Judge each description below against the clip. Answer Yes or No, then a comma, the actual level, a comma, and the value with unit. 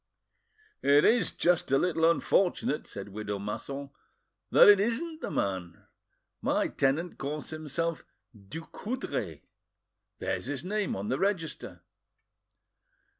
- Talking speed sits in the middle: No, slow, 115 wpm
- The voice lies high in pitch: No, medium, 155 Hz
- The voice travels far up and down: Yes, wide, 8.9 semitones